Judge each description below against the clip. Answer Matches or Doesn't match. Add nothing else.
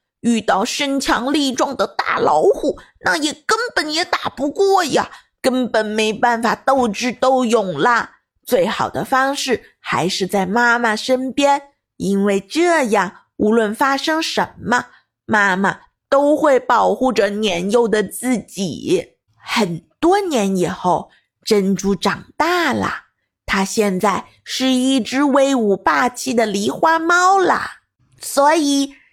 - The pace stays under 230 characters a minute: Matches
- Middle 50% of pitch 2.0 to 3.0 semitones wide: Doesn't match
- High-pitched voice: Matches